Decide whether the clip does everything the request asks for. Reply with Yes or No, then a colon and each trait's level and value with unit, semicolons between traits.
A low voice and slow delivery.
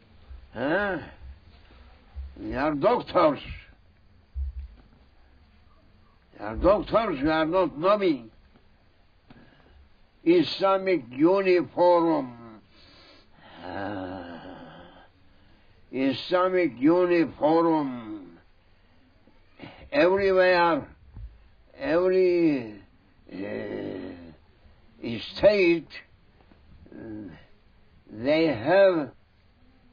Yes: low, 105 Hz; slow, 45 wpm